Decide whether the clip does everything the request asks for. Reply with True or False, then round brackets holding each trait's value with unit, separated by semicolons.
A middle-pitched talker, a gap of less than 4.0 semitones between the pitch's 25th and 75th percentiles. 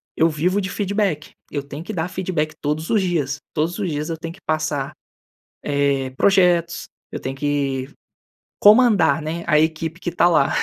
True (160 Hz; 3.4 semitones)